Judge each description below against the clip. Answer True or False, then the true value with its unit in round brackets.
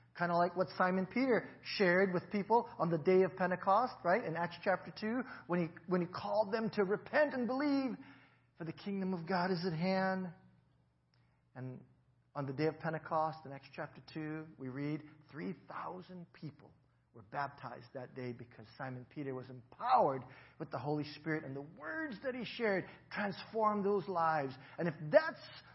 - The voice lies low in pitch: False (170 Hz)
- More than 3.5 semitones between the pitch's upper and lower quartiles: True (5.3 semitones)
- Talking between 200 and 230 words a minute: False (175 wpm)